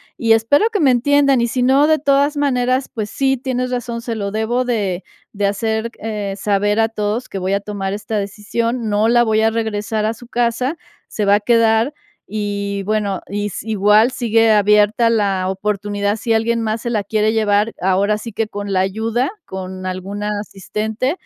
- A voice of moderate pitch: No, high, 220 Hz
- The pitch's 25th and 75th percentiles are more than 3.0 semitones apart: No, narrow, 2.5 semitones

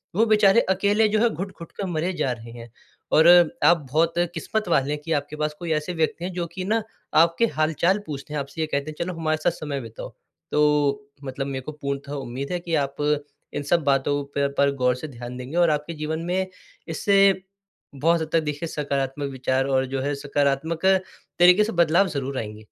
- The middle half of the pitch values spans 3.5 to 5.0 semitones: Yes, average, 3.8 semitones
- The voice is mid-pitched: Yes, medium, 155 Hz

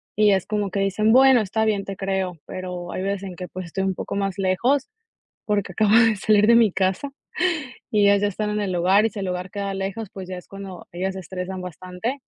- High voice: Yes, high, 195 Hz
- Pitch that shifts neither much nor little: No, narrow, 2.3 semitones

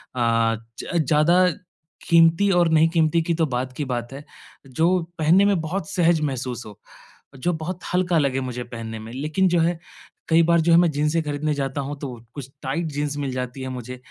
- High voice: No, medium, 150 Hz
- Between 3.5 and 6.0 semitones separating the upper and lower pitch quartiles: Yes, average, 4.5 semitones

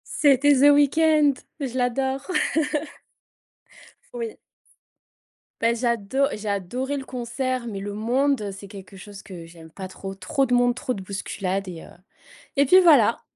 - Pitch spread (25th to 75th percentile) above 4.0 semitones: Yes, wide, 5.6 semitones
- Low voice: No, high, 240 Hz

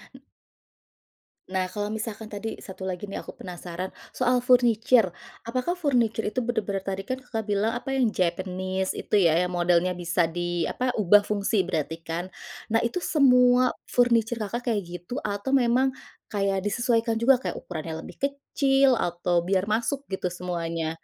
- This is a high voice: Yes, high, 205 Hz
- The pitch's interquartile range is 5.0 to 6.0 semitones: Yes, average, 5.3 semitones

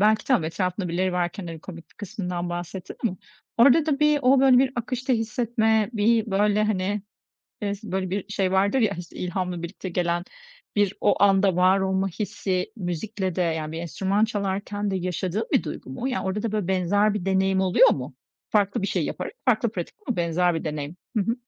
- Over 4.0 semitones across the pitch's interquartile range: No, average, 3.0 semitones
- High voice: Yes, high, 195 Hz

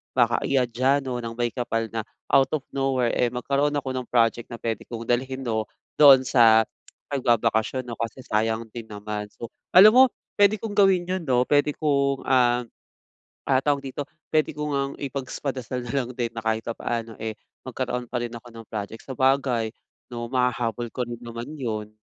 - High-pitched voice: No, low, 125 Hz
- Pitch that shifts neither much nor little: Yes, average, 3.0 semitones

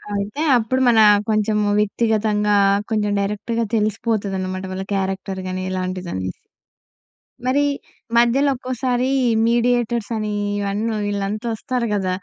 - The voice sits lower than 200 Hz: No, high, 215 Hz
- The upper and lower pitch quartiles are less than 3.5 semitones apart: Yes, average, 3.1 semitones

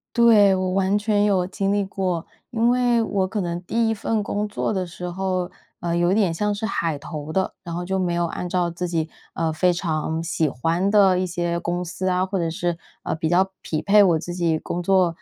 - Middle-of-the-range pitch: Yes, medium, 180 Hz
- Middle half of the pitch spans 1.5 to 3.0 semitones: Yes, average, 2.7 semitones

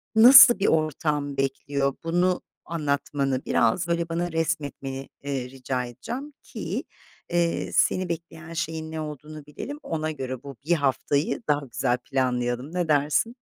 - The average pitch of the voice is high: No, medium, 150 Hz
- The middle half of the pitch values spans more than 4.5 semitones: No, average, 3.6 semitones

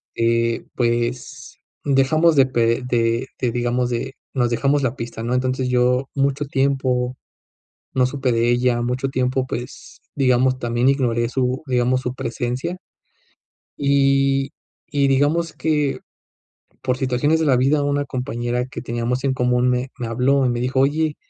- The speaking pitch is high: No, low, 130 Hz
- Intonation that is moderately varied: No, narrow, 2.1 semitones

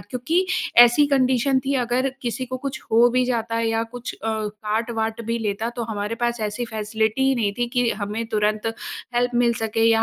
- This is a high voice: Yes, high, 230 Hz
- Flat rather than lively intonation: Yes, narrow, 2.0 semitones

